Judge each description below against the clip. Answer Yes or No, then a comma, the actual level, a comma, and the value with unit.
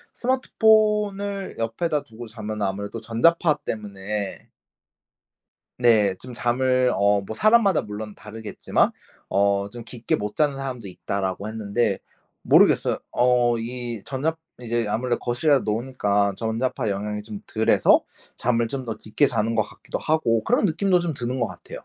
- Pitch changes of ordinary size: Yes, average, 4.4 semitones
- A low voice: Yes, low, 115 Hz